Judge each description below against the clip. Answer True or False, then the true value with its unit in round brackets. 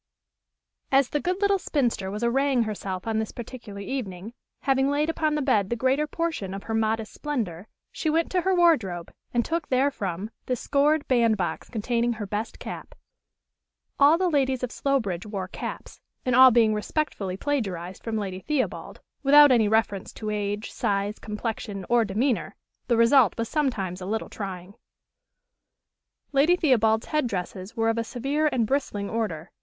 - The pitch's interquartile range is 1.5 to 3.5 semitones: False (5.3 semitones)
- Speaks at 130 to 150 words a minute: False (165 wpm)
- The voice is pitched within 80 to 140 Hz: False (230 Hz)